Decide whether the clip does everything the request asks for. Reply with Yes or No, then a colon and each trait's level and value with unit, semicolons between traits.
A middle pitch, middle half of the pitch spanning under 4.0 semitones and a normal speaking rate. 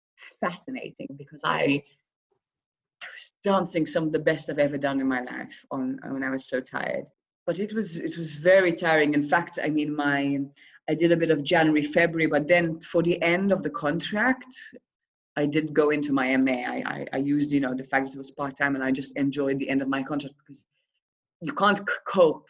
No: medium, 150 Hz; average, 3.5 semitones; fast, 220 wpm